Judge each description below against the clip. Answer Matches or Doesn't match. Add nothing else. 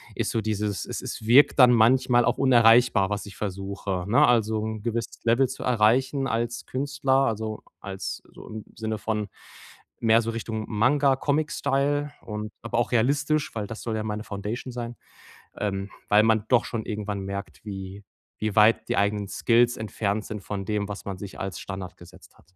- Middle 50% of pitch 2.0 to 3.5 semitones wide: Matches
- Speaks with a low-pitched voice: Matches